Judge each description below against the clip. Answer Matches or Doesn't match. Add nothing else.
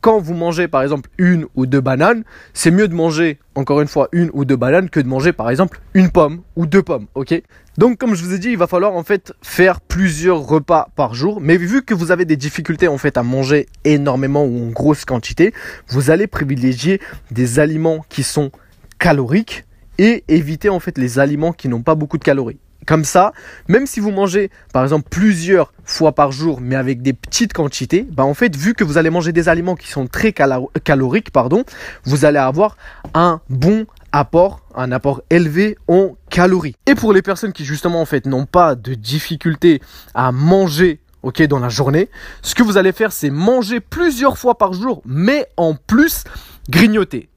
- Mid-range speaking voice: Matches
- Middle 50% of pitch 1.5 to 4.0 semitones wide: Doesn't match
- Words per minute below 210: Matches